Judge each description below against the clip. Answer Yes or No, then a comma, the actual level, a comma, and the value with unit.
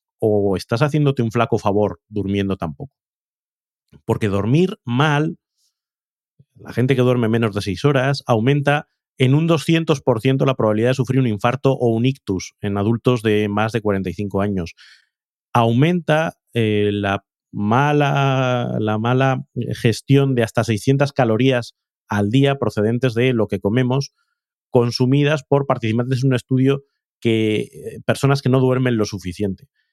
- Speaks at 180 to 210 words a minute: No, average, 140 wpm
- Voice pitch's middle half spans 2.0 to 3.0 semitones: No, average, 4.3 semitones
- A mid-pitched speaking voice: No, low, 125 Hz